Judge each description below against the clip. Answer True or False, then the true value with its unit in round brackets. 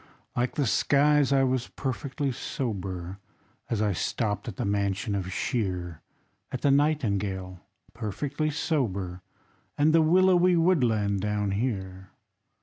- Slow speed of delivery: True (125 wpm)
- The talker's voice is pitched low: True (115 Hz)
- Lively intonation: True (6.6 semitones)